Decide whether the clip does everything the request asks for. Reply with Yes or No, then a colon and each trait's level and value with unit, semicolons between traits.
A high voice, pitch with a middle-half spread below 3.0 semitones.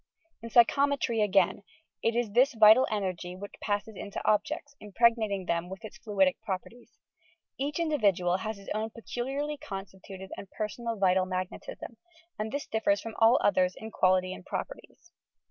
No: high, 215 Hz; average, 3.9 semitones